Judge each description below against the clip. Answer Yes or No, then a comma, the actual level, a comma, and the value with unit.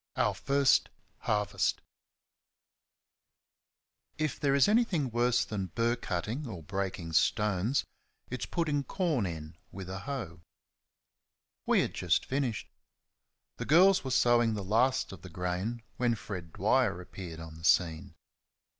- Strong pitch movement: Yes, wide, 6.6 semitones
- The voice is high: No, low, 110 Hz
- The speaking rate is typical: No, slow, 130 wpm